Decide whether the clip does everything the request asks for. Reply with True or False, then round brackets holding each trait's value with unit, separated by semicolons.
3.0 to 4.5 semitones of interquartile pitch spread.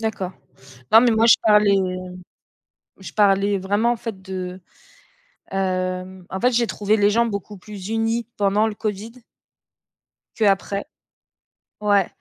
False (2.5 semitones)